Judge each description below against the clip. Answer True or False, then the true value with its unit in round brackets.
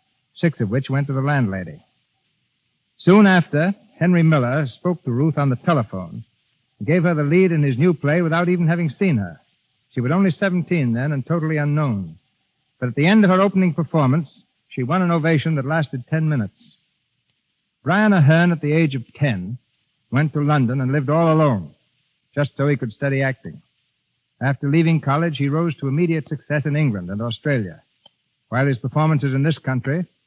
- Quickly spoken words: False (185 wpm)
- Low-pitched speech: False (145 Hz)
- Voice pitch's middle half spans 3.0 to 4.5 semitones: True (4.2 semitones)